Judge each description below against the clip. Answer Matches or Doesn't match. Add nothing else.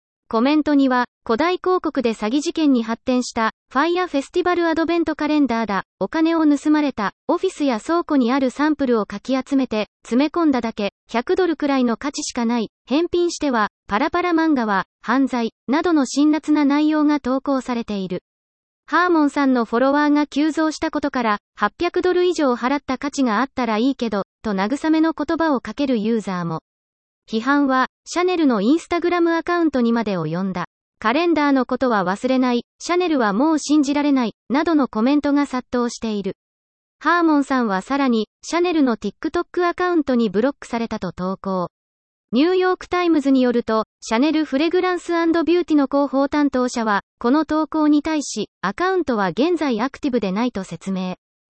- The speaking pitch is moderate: Doesn't match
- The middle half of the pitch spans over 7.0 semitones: Doesn't match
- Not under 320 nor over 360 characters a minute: Doesn't match